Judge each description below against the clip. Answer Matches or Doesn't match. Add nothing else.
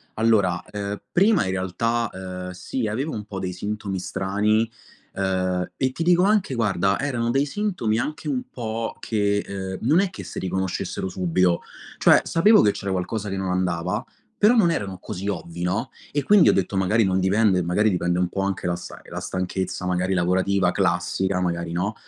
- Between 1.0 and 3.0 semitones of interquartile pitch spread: Doesn't match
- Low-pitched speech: Matches